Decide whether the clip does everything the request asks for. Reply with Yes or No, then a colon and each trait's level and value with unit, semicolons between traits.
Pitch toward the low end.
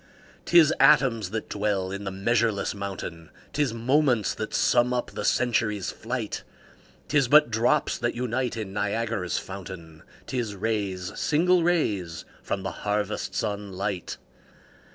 Yes: low, 110 Hz